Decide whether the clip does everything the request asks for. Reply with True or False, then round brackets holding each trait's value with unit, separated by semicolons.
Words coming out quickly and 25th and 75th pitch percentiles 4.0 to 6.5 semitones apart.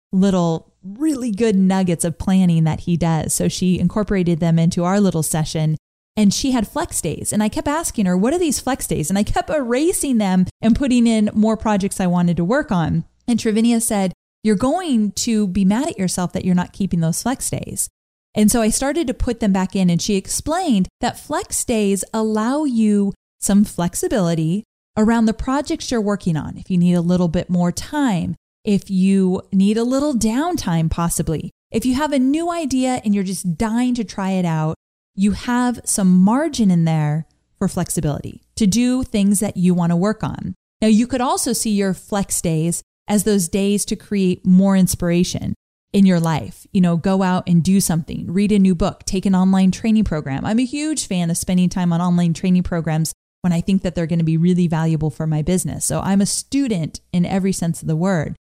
True (210 wpm; 4.3 semitones)